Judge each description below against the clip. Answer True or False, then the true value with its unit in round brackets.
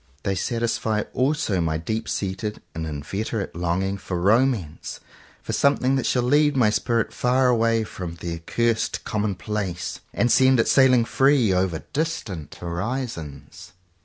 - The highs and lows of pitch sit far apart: True (5.8 semitones)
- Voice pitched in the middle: False (110 Hz)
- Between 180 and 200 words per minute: False (140 wpm)